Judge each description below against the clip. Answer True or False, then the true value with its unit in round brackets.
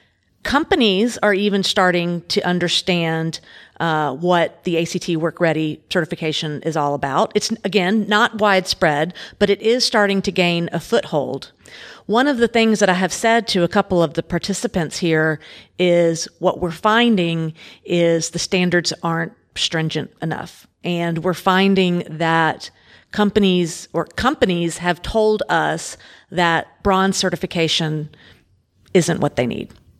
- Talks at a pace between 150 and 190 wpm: False (140 wpm)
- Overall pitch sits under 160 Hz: False (175 Hz)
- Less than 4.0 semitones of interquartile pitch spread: True (3.6 semitones)